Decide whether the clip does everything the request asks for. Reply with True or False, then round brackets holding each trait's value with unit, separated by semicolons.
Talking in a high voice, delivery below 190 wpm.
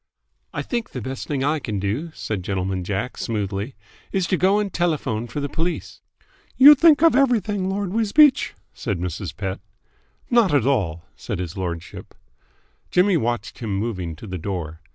False (125 Hz; 170 wpm)